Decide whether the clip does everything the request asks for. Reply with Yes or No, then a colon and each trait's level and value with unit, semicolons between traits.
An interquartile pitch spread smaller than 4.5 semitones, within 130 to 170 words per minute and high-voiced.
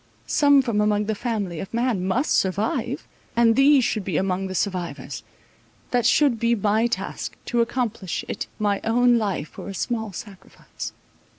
Yes: average, 3.6 semitones; average, 160 wpm; high, 220 Hz